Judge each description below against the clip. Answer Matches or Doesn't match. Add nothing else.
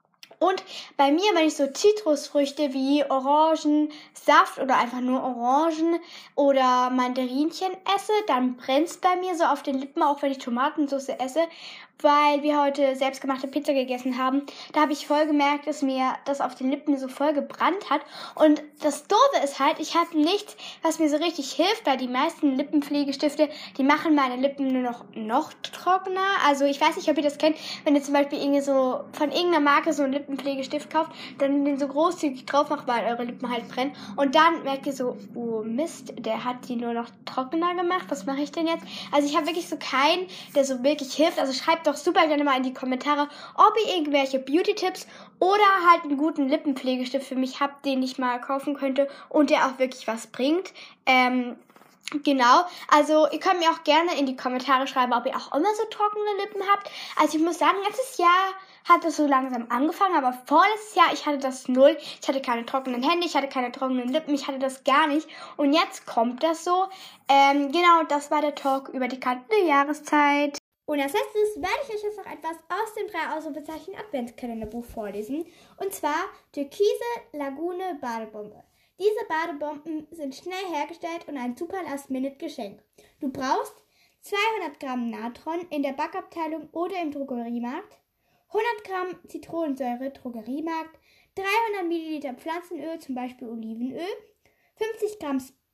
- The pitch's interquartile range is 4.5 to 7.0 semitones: Doesn't match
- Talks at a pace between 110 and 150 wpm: Doesn't match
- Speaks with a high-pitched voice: Matches